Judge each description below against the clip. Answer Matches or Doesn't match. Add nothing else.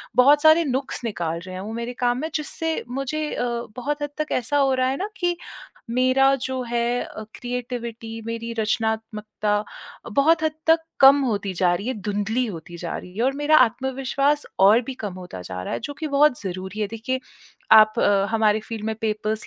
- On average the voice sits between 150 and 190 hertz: Doesn't match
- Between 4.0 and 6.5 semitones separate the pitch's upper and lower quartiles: Matches